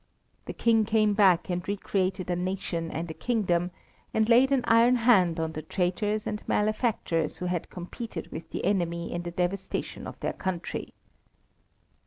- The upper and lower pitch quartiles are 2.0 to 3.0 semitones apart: No, average, 3.8 semitones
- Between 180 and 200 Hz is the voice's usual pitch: Yes, medium, 185 Hz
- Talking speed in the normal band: Yes, average, 170 wpm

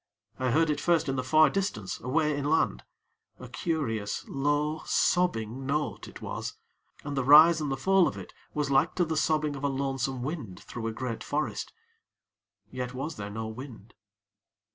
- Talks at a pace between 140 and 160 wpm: No, average, 175 wpm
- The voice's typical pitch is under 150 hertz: Yes, medium, 140 Hz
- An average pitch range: Yes, average, 3.7 semitones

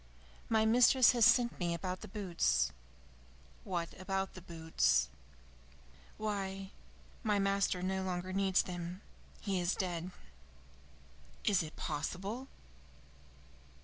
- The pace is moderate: No, slow, 110 wpm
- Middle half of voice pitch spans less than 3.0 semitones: Yes, narrow, 2.5 semitones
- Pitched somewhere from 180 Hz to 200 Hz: Yes, high, 190 Hz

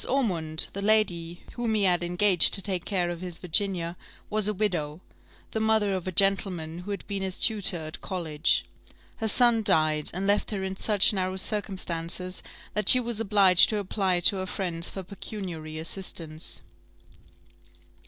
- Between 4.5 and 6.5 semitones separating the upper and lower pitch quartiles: No, average, 3.2 semitones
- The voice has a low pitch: No, high, 190 Hz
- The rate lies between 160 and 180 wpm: Yes, average, 165 wpm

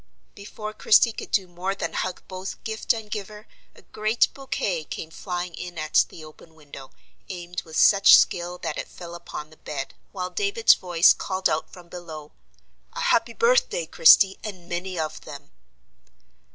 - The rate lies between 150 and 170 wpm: Yes, average, 165 wpm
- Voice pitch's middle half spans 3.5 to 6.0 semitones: Yes, average, 3.8 semitones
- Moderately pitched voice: Yes, medium, 180 Hz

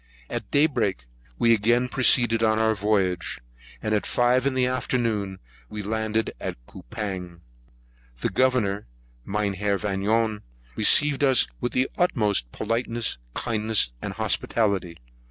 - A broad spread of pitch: No, average, 3.3 semitones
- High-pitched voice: No, low, 110 Hz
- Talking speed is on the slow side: Yes, slow, 125 wpm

